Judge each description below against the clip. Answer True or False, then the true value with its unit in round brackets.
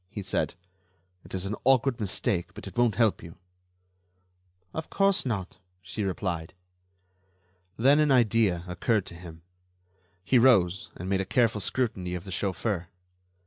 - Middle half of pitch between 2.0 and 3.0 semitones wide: False (5.0 semitones)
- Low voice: True (100 Hz)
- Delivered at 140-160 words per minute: True (145 wpm)